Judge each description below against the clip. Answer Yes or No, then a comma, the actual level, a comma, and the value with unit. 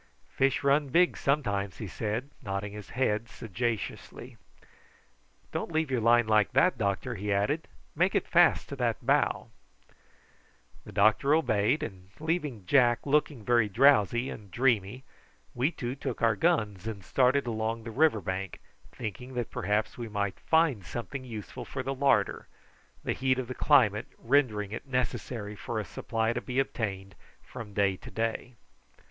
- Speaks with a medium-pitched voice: No, low, 115 Hz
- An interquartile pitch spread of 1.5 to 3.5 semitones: No, average, 4.4 semitones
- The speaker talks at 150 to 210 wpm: Yes, average, 155 wpm